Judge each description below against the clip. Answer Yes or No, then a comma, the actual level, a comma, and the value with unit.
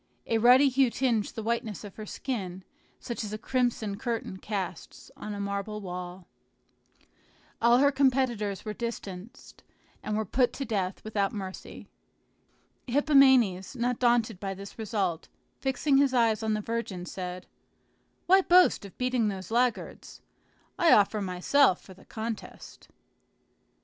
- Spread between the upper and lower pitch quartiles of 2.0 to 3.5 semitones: No, average, 4.0 semitones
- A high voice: Yes, high, 220 Hz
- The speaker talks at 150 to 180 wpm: No, average, 140 wpm